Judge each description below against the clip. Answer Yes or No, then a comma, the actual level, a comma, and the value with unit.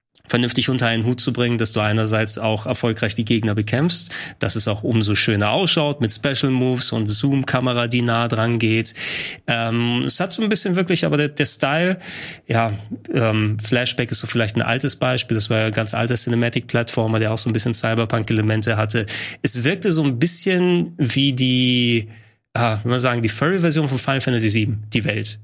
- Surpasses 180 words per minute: Yes, fast, 190 wpm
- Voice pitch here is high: No, low, 120 Hz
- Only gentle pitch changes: No, average, 3.2 semitones